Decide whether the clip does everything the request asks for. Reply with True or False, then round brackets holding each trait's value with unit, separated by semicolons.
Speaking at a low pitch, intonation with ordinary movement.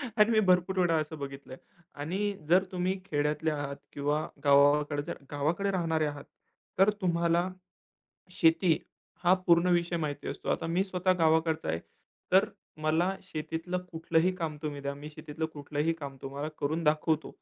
False (160 Hz; 3.2 semitones)